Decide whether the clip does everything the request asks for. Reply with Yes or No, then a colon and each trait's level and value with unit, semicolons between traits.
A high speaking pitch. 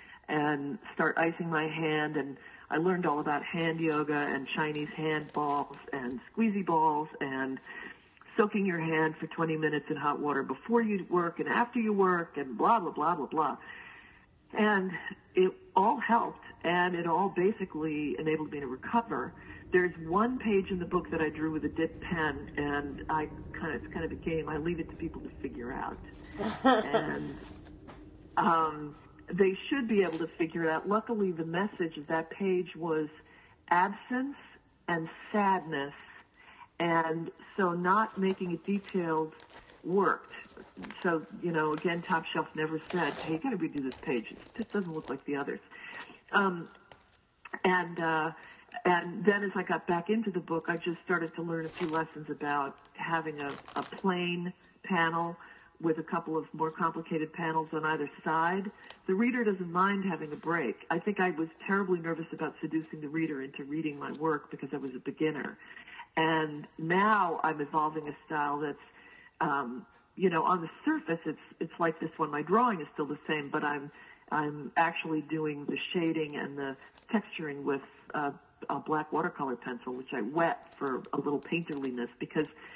No: medium, 160 Hz